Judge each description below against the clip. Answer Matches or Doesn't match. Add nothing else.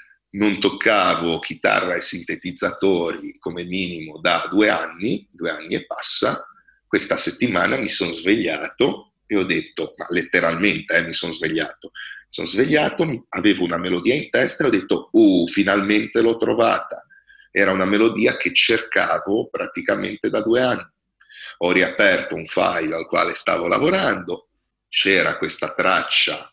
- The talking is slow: Doesn't match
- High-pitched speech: Matches